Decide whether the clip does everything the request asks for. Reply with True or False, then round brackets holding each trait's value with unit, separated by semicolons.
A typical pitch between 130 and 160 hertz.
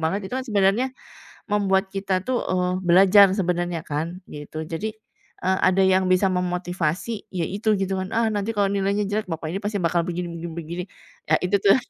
False (190 Hz)